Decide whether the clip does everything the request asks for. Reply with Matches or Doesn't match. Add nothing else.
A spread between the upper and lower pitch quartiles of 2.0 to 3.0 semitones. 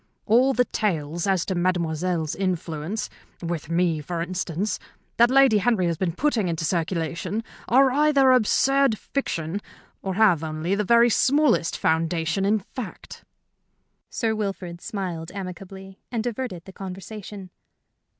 Doesn't match